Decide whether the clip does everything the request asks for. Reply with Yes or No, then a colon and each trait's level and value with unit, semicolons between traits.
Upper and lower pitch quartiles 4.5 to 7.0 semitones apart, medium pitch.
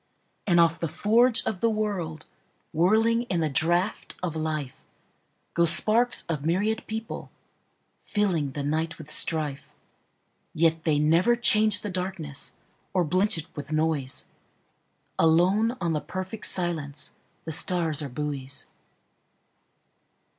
Yes: average, 4.9 semitones; medium, 170 Hz